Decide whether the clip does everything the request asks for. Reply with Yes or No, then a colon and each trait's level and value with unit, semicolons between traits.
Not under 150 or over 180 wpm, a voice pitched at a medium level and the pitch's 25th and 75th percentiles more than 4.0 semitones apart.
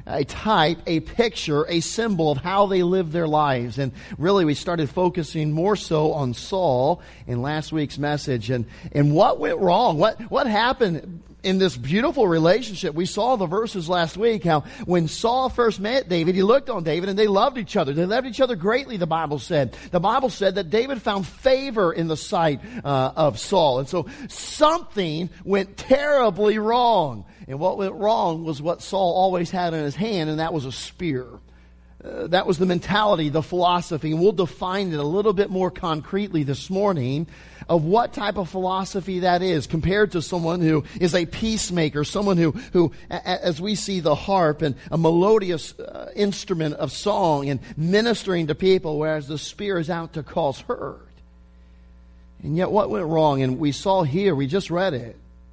No: average, 190 wpm; medium, 175 Hz; average, 4.5 semitones